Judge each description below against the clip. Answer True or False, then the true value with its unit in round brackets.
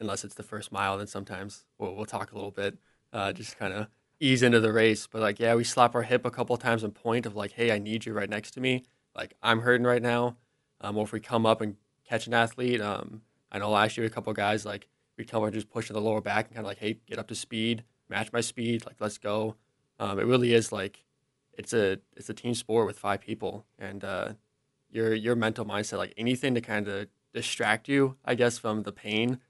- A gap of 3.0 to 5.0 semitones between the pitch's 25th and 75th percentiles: False (2.4 semitones)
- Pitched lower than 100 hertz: False (110 Hz)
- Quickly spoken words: True (250 wpm)